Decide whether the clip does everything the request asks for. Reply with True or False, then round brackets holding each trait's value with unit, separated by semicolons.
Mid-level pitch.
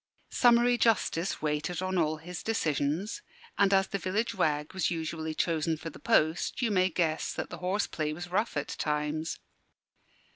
True (170 Hz)